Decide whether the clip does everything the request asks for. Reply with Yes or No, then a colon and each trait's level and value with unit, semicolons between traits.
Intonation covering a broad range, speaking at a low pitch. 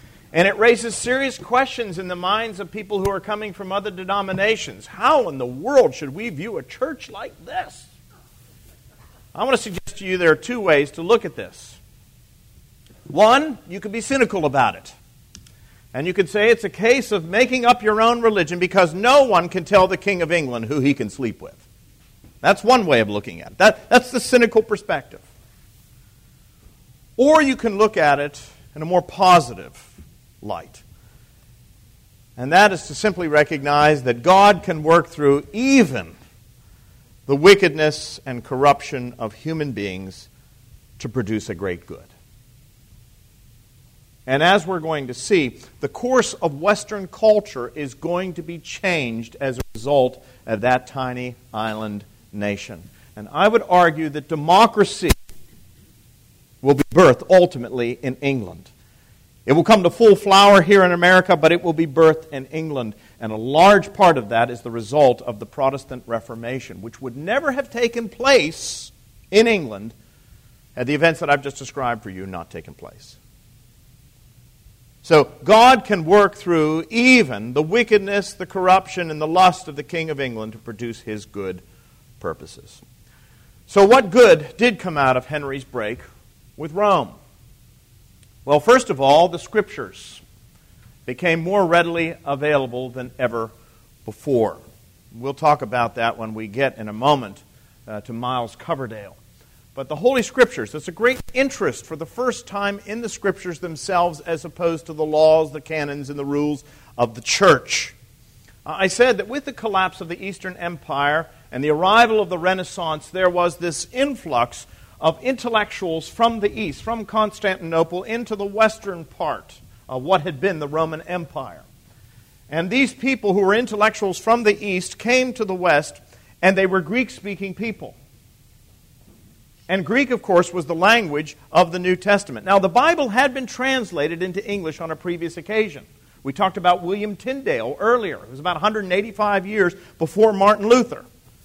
No: wide, 8.4 semitones; medium, 160 Hz